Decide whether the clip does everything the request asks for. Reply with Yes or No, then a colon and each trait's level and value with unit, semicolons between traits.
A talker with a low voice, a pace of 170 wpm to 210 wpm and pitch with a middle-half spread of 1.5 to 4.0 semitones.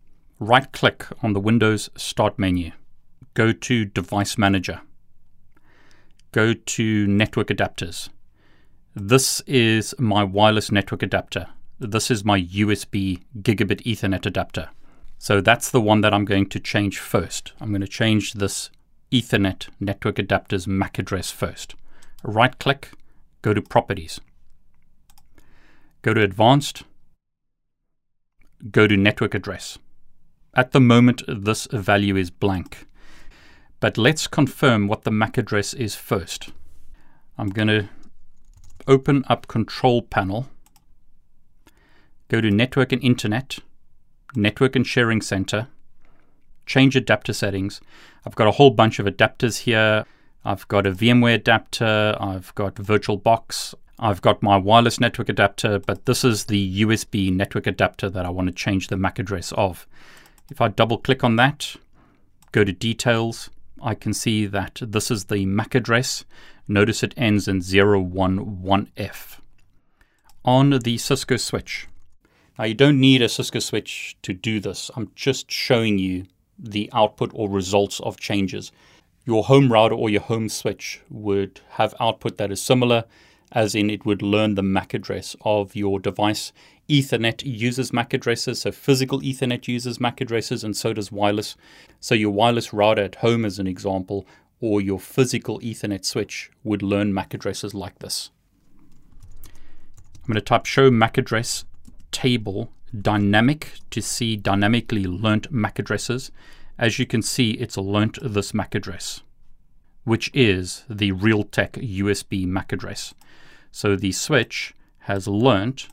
No: low, 105 Hz; average, 140 wpm; average, 3.2 semitones